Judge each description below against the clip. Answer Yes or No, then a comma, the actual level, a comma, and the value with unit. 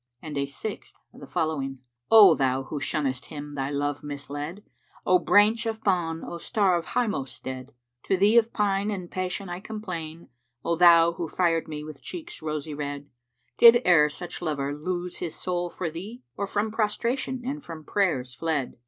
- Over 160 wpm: Yes, average, 185 wpm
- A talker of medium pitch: Yes, medium, 170 Hz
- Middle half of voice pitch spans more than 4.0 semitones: Yes, wide, 5.6 semitones